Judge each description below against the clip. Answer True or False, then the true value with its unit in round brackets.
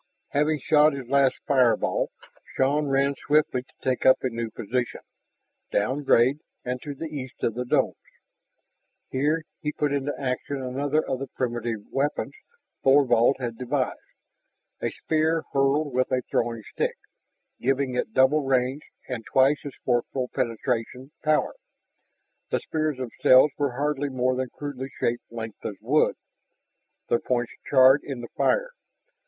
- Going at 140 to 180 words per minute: True (145 wpm)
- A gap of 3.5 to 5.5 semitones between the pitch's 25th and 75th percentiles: False (2.5 semitones)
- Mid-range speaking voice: False (130 Hz)